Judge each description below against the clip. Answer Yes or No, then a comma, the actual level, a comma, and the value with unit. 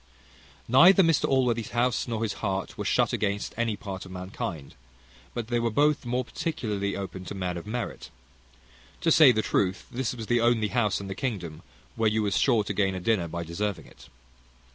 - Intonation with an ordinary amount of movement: Yes, average, 3.9 semitones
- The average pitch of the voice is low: Yes, low, 110 Hz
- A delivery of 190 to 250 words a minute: Yes, average, 195 wpm